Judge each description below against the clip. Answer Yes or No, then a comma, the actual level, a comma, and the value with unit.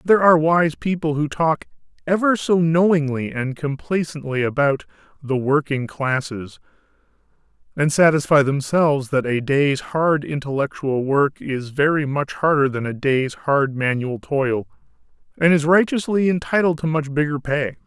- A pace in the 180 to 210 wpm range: No, average, 140 wpm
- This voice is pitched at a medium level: Yes, medium, 145 Hz